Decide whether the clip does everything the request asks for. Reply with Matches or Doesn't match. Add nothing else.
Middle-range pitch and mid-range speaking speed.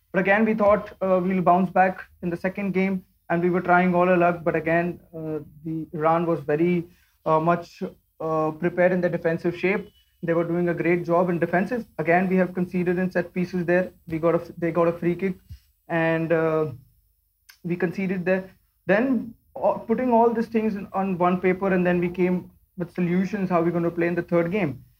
Doesn't match